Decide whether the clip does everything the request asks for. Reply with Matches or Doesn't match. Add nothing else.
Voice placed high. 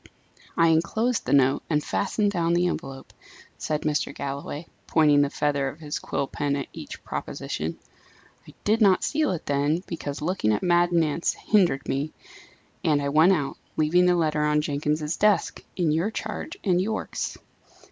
Doesn't match